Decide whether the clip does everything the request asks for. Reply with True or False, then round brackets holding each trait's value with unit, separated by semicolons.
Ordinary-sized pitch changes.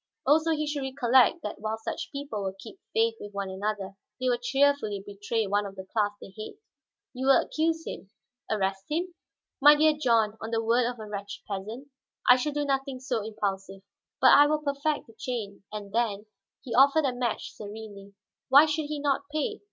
False (5.7 semitones)